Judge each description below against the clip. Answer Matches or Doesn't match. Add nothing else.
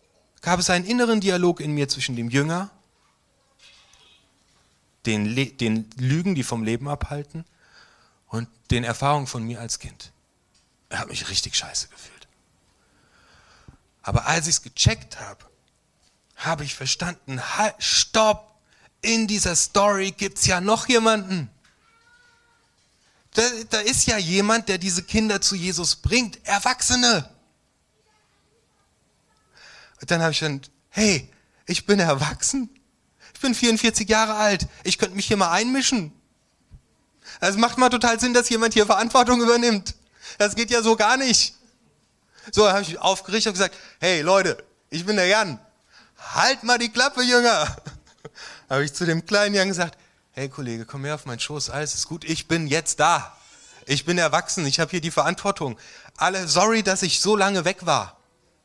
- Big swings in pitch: Matches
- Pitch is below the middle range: Doesn't match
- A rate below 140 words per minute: Doesn't match